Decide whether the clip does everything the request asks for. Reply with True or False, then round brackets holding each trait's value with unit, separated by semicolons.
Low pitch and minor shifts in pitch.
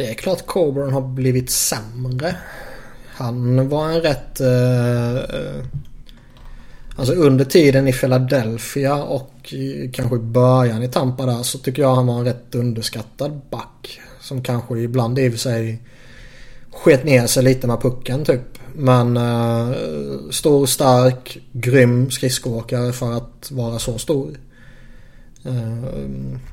True (130 Hz; 1.6 semitones)